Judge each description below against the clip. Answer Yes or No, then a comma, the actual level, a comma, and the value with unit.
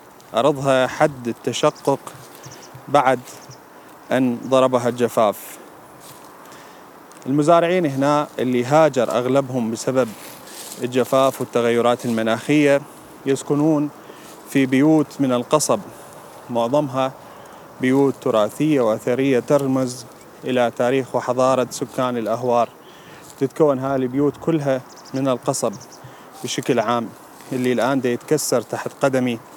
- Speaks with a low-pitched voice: Yes, low, 130 Hz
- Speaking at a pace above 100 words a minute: No, average, 90 wpm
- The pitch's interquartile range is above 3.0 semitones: No, narrow, 2.4 semitones